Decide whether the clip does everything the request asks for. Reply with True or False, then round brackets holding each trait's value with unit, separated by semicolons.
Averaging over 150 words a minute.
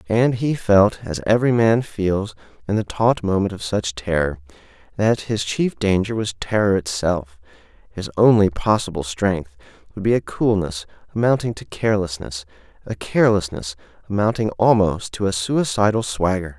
False (145 wpm)